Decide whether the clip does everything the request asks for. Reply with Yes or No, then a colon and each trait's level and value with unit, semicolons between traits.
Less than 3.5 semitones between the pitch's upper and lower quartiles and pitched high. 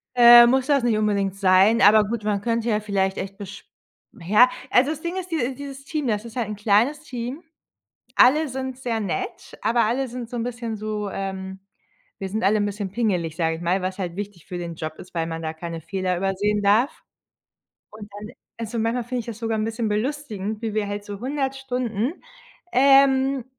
No: average, 4.2 semitones; high, 220 Hz